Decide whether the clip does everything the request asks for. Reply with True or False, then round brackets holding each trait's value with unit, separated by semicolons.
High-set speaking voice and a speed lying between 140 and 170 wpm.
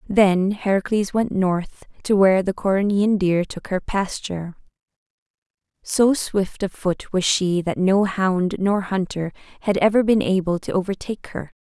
True (195 Hz; 155 wpm)